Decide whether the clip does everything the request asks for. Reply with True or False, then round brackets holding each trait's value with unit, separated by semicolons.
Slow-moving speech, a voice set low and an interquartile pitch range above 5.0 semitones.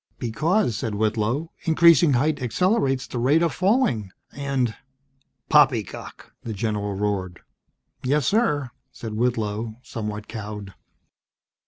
True (115 wpm; 120 Hz; 5.5 semitones)